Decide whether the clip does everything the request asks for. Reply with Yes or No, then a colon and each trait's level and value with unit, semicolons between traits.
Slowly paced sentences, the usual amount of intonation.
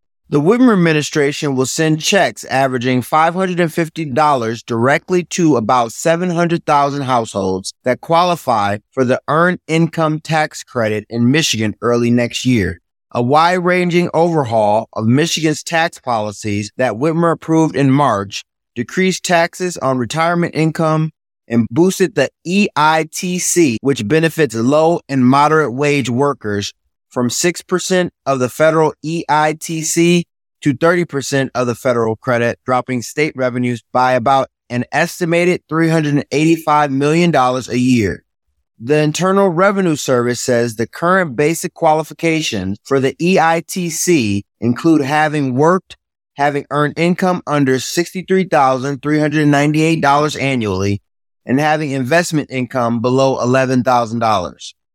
Yes: slow, 115 wpm; average, 4.9 semitones